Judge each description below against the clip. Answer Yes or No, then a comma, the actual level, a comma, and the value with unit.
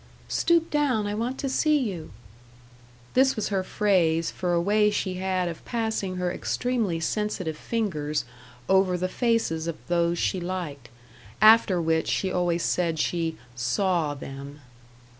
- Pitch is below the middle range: No, medium, 185 Hz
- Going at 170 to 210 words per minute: No, average, 145 wpm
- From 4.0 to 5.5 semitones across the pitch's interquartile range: Yes, average, 4.5 semitones